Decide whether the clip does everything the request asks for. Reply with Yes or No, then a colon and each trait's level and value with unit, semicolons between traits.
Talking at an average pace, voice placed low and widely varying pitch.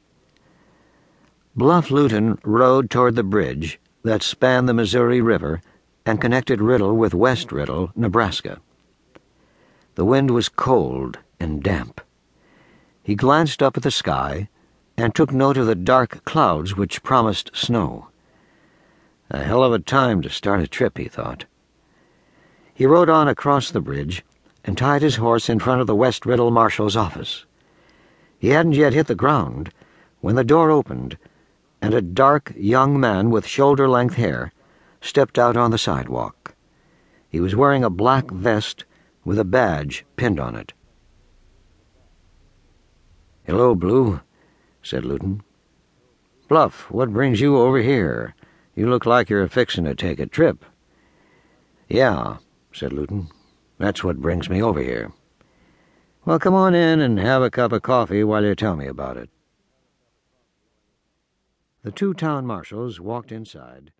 Yes: average, 145 wpm; low, 115 Hz; wide, 6.0 semitones